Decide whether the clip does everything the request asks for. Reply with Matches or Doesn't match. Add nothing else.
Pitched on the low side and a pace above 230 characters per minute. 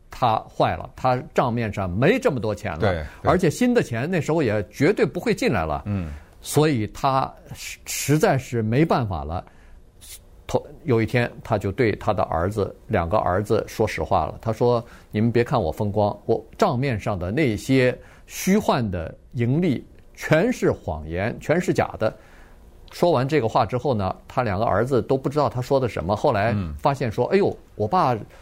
Matches